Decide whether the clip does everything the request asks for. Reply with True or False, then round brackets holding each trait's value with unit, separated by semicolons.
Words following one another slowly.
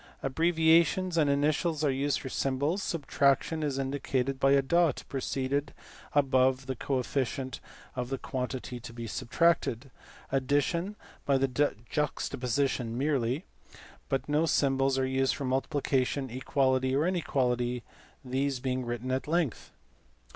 True (125 wpm)